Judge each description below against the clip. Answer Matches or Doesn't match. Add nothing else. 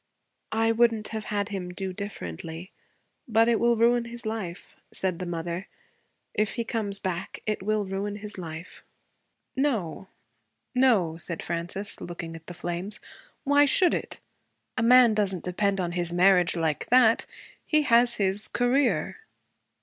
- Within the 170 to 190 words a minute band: Doesn't match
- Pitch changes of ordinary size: Matches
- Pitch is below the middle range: Doesn't match